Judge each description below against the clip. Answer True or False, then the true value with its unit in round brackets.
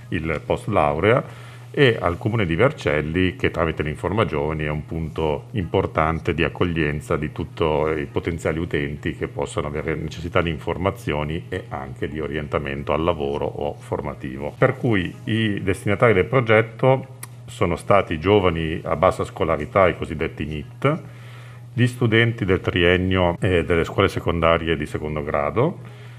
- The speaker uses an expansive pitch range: True (6.1 semitones)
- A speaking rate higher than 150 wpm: False (140 wpm)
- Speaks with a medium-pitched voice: False (90 Hz)